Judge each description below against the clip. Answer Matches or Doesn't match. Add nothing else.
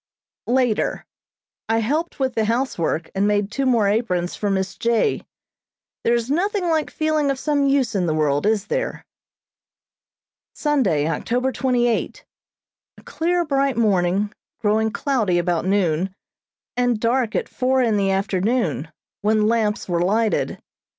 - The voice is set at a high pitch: Matches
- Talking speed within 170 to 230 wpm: Doesn't match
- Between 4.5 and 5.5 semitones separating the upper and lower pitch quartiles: Matches